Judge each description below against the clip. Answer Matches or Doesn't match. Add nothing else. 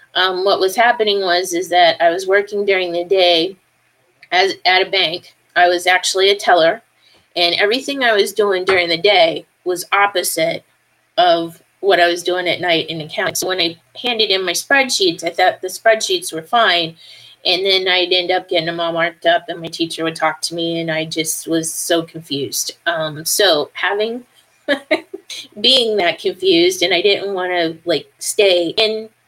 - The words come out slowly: Doesn't match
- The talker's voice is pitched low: Doesn't match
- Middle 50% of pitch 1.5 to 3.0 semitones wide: Doesn't match